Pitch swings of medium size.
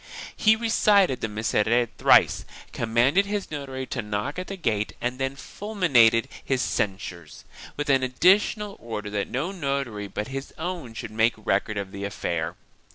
No: wide, 7.6 semitones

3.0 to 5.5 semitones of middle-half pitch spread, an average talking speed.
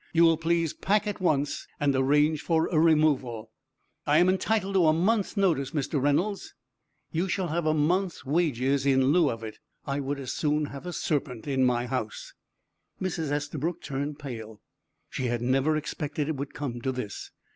Yes: average, 3.9 semitones; average, 180 wpm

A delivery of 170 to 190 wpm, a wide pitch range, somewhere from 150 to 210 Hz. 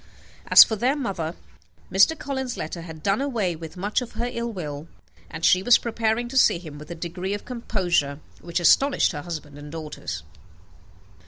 Yes: average, 175 wpm; wide, 6.6 semitones; medium, 185 Hz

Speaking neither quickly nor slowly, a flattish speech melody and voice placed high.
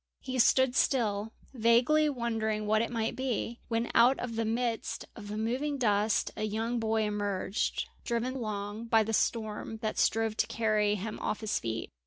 Yes: average, 175 wpm; narrow, 1.9 semitones; high, 225 Hz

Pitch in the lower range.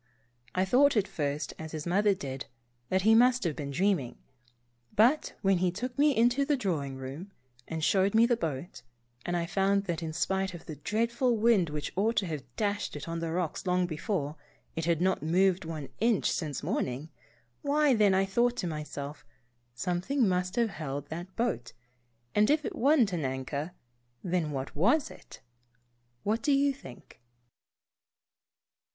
No: medium, 185 Hz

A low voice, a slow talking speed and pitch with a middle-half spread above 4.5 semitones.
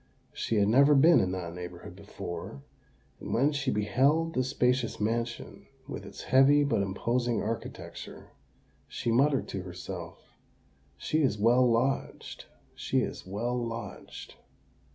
Yes: low, 120 Hz; slow, 130 wpm; average, 5.1 semitones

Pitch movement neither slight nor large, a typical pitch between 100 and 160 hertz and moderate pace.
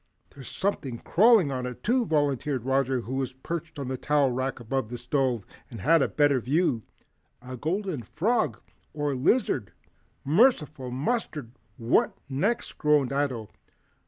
Yes: average, 4.0 semitones; low, 135 Hz; average, 150 wpm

